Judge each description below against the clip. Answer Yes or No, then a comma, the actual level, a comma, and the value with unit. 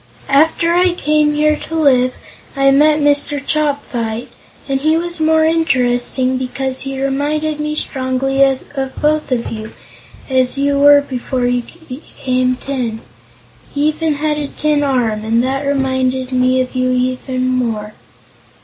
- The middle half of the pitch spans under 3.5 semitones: Yes, average, 2.8 semitones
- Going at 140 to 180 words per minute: Yes, average, 150 wpm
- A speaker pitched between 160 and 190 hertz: No, very high, 270 Hz